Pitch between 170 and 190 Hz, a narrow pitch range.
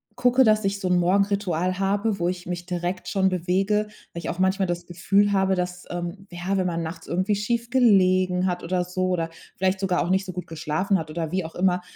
Yes: medium, 185 Hz; narrow, 2.0 semitones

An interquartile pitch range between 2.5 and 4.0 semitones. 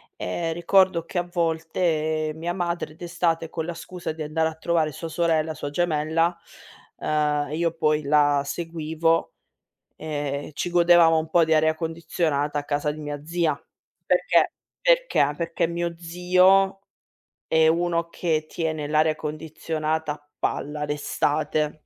No: narrow, 2.0 semitones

